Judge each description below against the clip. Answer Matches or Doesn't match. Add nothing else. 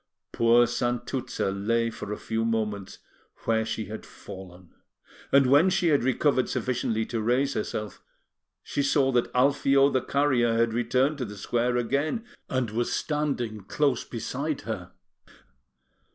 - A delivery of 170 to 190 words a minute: Doesn't match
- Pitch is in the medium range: Doesn't match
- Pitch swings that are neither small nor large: Matches